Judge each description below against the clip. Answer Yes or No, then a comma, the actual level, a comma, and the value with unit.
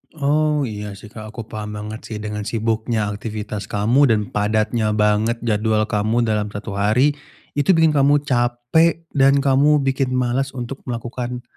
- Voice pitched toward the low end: Yes, low, 115 Hz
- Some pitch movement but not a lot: Yes, average, 4.2 semitones